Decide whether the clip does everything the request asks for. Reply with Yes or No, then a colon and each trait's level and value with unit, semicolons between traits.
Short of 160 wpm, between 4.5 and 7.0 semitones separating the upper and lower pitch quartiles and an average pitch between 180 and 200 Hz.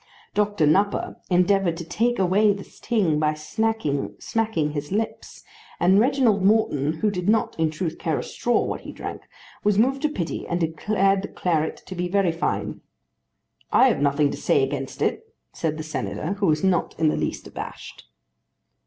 No: average, 175 wpm; average, 5.1 semitones; medium, 185 Hz